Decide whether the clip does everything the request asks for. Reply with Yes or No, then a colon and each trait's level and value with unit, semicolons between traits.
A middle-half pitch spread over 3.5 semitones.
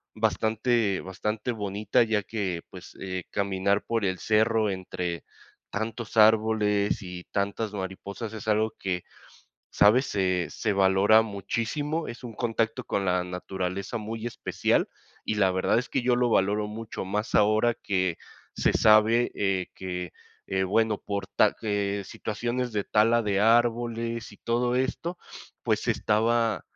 No: average, 2.7 semitones